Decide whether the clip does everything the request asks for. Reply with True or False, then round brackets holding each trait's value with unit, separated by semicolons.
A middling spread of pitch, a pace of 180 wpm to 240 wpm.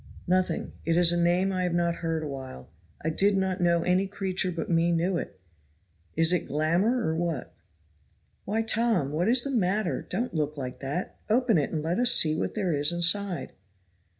True (3.3 semitones; 195 wpm)